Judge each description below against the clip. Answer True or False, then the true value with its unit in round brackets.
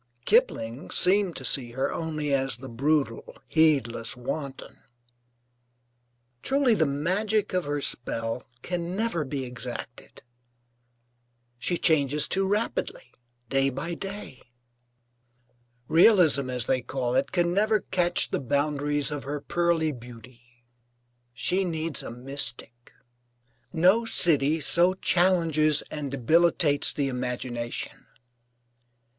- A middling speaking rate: False (110 wpm)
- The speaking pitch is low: False (150 Hz)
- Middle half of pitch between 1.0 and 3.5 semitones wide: False (5.3 semitones)